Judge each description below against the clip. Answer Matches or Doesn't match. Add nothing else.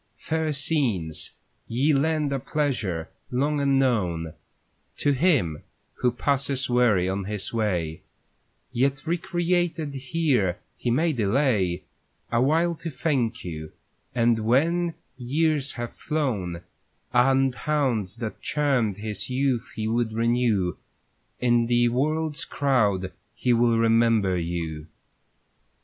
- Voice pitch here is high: Doesn't match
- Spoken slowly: Matches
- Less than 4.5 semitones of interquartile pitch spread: Doesn't match